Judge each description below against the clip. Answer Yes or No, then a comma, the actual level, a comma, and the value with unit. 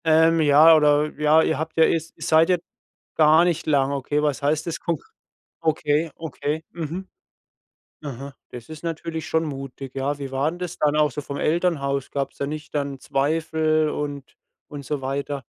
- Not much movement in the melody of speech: Yes, narrow, 2.3 semitones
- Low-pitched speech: No, medium, 150 Hz